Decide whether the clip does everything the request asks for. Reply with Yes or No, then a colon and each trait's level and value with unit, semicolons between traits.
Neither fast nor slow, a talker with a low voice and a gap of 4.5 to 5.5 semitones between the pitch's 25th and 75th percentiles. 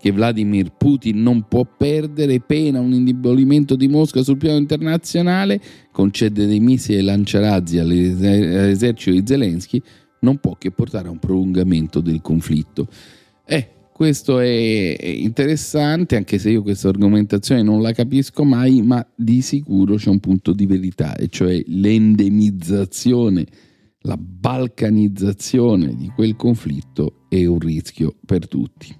Yes: average, 130 wpm; low, 110 Hz; average, 4.9 semitones